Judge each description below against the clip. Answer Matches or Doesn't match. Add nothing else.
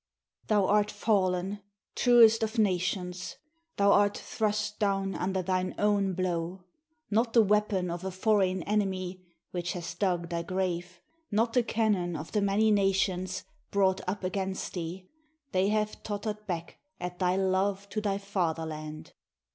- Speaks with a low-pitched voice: Doesn't match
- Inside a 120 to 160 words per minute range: Matches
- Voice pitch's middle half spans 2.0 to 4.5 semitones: Matches